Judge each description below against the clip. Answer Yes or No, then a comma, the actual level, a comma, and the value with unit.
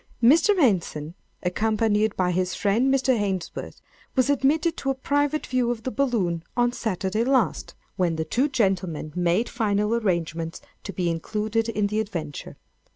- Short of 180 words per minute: Yes, average, 150 wpm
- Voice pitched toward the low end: No, high, 215 Hz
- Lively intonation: Yes, wide, 6.0 semitones